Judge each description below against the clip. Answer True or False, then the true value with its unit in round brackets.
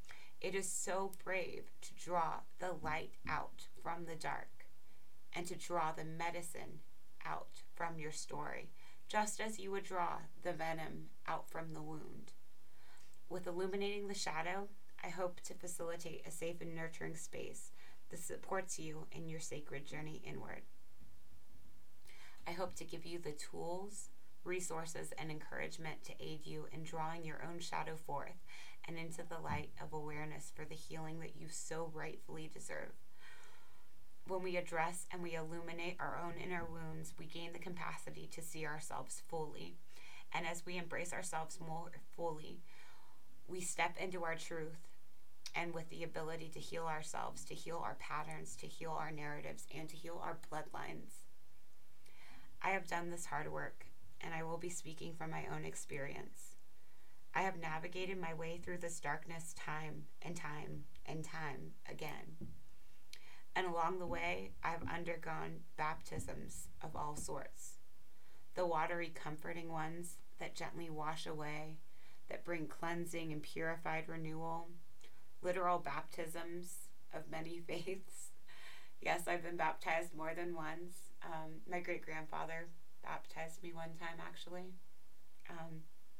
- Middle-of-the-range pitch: True (165 Hz)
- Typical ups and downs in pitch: False (1.8 semitones)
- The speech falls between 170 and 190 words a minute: False (145 wpm)